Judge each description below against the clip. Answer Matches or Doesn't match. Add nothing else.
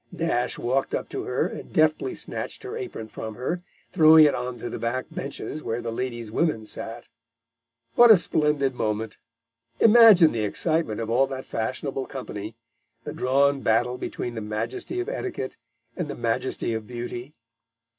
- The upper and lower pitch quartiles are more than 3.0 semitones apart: Matches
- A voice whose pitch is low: Matches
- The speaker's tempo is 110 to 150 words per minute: Doesn't match